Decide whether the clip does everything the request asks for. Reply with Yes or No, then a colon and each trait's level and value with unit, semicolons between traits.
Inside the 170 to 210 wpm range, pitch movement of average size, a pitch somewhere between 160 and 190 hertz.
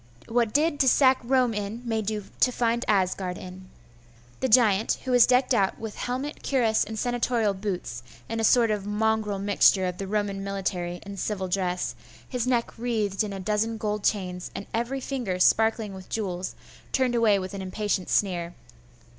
No: average, 180 wpm; average, 3.6 semitones; high, 210 Hz